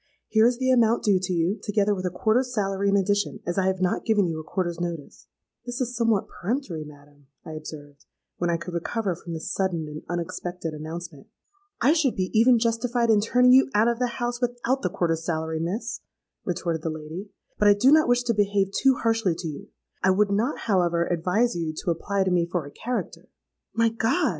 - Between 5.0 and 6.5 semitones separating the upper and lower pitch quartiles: Yes, wide, 5.4 semitones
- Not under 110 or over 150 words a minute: No, fast, 205 wpm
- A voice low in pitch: No, high, 195 Hz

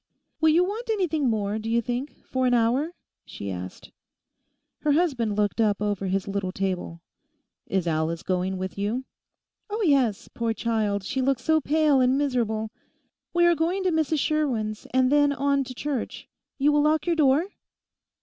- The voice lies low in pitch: No, very high, 255 Hz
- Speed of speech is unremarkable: Yes, average, 170 wpm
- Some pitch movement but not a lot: No, wide, 6.6 semitones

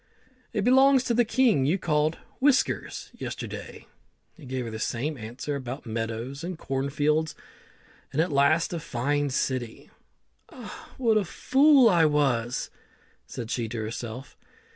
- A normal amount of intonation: No, wide, 7.9 semitones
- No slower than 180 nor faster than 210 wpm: No, average, 145 wpm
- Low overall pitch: No, medium, 145 Hz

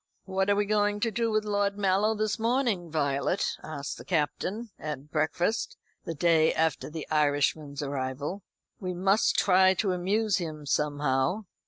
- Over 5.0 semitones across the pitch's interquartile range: Yes, wide, 5.5 semitones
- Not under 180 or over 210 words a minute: No, average, 155 wpm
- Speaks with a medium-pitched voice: Yes, medium, 180 Hz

